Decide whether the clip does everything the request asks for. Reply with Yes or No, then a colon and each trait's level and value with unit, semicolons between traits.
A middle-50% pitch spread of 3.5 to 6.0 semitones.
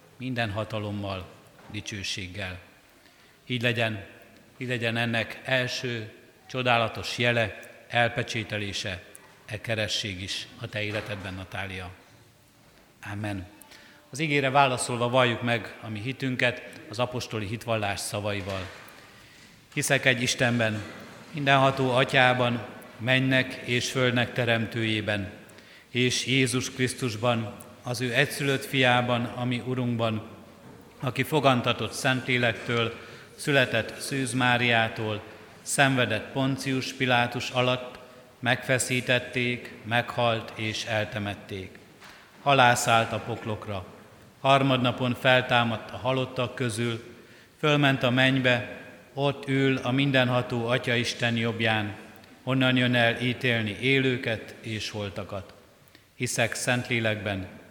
No: average, 2.8 semitones